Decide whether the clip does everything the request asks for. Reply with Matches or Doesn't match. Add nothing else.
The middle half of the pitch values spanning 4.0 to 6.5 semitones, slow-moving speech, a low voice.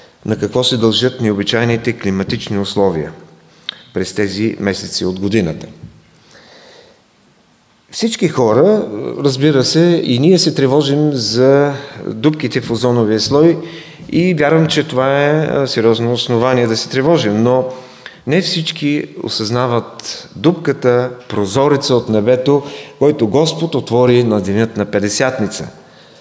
Matches